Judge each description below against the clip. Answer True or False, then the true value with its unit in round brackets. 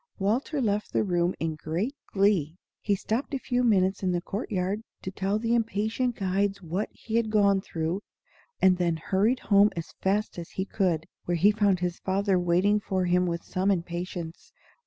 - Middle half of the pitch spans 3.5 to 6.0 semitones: False (3.0 semitones)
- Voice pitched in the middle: False (195 Hz)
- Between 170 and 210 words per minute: True (185 wpm)